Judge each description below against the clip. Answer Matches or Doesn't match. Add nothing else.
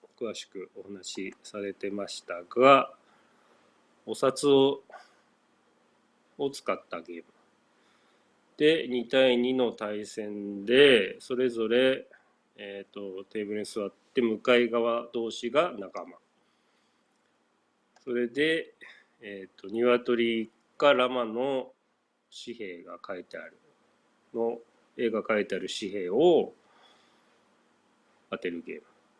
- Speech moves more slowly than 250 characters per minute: Matches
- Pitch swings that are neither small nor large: Matches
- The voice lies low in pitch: Matches